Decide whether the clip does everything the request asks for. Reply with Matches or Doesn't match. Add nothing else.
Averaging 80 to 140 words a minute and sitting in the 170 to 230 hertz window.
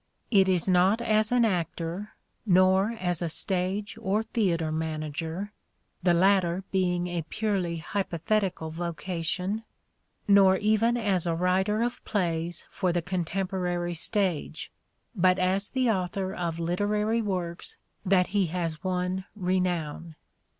Matches